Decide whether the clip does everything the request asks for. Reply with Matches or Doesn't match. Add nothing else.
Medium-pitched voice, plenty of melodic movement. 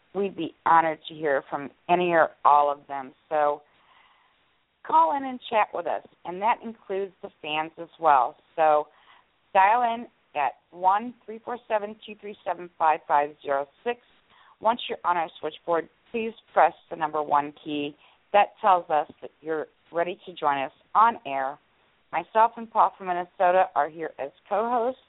Matches